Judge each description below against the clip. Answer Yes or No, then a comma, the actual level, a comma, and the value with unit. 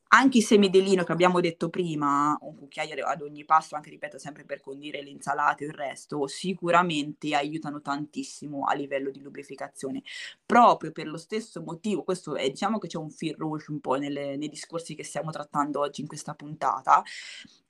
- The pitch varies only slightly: No, average, 3.2 semitones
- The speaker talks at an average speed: No, fast, 190 wpm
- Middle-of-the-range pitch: Yes, medium, 150 Hz